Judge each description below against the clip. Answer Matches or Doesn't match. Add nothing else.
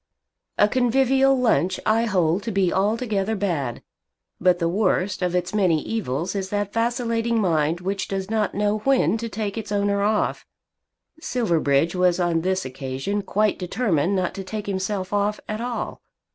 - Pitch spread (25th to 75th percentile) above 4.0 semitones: Doesn't match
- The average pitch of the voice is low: Doesn't match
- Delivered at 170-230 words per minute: Doesn't match